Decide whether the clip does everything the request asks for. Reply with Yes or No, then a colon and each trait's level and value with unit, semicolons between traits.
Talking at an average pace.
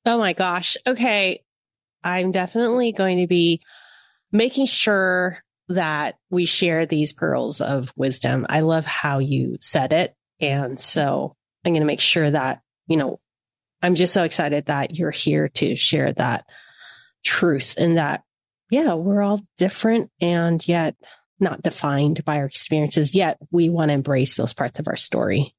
Yes: average, 160 wpm